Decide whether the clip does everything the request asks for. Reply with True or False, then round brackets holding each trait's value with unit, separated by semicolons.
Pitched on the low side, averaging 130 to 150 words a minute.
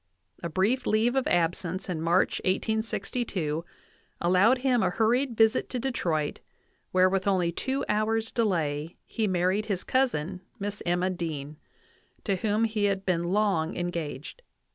False (190 Hz; 145 wpm)